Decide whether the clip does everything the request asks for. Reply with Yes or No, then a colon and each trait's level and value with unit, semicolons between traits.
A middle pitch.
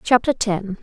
No: high, 215 Hz